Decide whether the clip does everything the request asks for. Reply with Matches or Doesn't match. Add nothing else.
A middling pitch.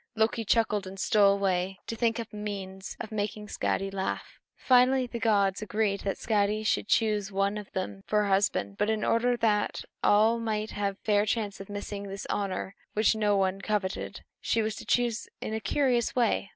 Doesn't match